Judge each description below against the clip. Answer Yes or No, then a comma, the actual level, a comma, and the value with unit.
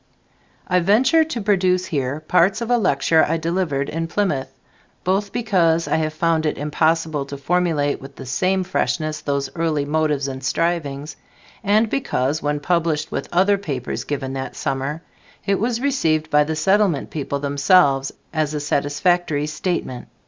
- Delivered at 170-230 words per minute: No, average, 155 wpm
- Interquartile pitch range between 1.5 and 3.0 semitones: No, average, 4.2 semitones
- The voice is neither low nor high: Yes, medium, 160 Hz